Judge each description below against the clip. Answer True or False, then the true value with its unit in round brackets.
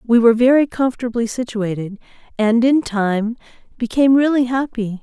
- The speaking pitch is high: True (235 Hz)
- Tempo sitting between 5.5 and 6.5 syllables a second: False (5.3 syllables/s)